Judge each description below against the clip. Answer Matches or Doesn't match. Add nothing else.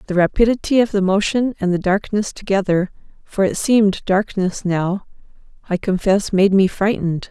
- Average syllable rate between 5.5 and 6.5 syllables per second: Doesn't match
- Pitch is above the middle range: Matches